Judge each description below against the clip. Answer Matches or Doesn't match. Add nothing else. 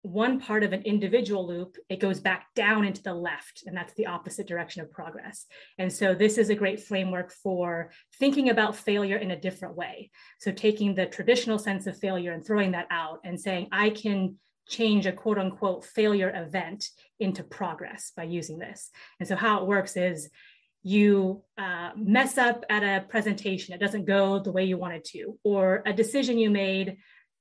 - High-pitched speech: Matches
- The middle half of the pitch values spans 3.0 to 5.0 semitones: Doesn't match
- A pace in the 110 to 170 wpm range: Doesn't match